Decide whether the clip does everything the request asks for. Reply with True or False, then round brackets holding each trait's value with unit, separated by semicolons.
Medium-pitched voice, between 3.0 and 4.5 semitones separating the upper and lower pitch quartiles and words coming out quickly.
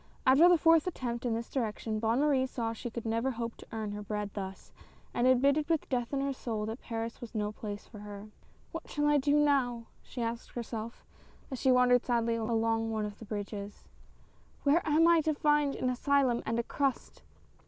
False (235 Hz; 3.8 semitones; 215 wpm)